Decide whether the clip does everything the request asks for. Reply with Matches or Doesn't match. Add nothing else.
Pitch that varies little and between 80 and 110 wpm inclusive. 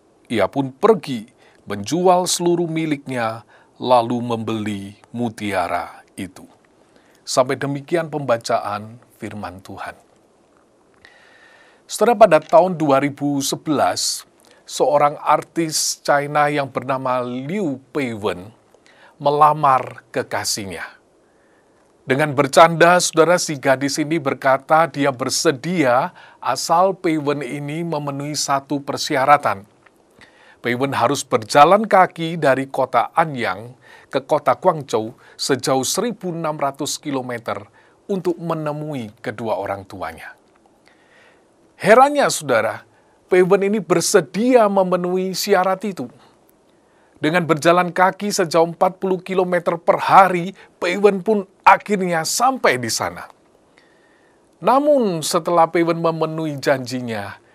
Doesn't match